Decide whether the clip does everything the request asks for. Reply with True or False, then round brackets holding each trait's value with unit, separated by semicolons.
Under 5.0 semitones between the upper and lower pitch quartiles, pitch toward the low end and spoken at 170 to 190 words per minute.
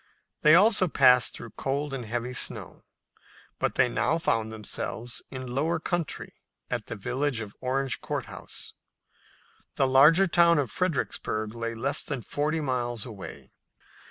False (4.4 semitones; 130 Hz; 145 wpm)